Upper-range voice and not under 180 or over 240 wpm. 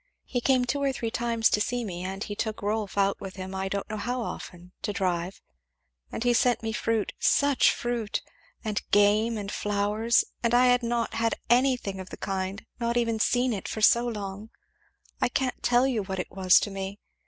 Yes: high, 220 Hz; fast, 205 wpm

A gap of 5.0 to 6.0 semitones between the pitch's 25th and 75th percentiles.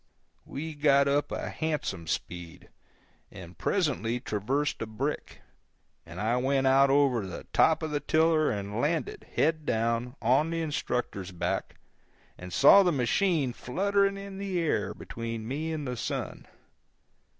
Yes: wide, 5.5 semitones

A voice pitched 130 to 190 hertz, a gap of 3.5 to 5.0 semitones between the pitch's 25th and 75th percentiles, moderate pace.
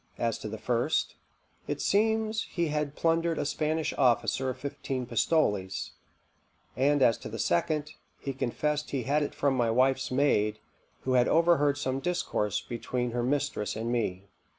Yes: low, 135 Hz; average, 4.1 semitones; average, 160 wpm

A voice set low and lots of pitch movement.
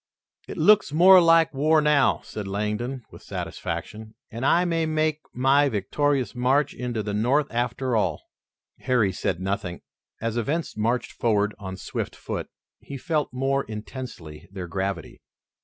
Yes: low, 125 Hz; wide, 5.7 semitones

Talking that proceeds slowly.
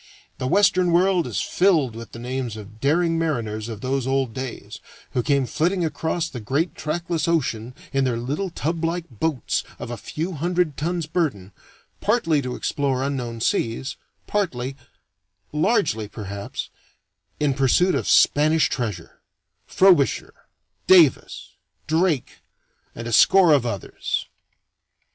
Yes: slow, 130 wpm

